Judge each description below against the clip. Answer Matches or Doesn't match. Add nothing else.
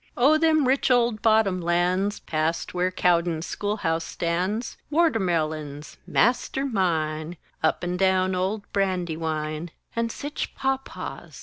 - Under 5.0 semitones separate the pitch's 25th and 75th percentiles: Doesn't match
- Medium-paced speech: Doesn't match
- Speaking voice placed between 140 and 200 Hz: Matches